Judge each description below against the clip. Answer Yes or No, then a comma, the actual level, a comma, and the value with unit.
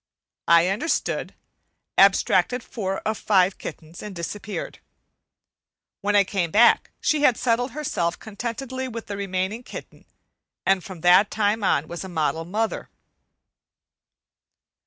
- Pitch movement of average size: Yes, average, 4.0 semitones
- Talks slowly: Yes, slow, 130 wpm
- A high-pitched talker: Yes, high, 200 Hz